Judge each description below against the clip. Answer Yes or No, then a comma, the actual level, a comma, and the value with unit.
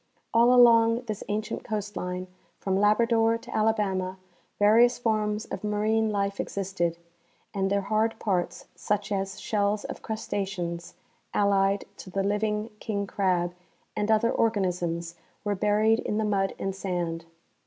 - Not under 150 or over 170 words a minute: No, average, 140 wpm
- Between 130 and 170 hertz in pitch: No, high, 205 Hz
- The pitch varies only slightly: Yes, narrow, 2.1 semitones